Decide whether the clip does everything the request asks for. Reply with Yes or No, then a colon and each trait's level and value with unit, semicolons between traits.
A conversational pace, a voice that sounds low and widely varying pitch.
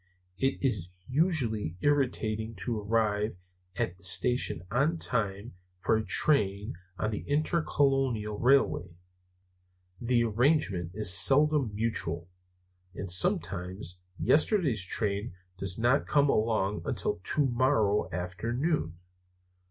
No: slow, 105 wpm; low, 110 Hz; wide, 5.7 semitones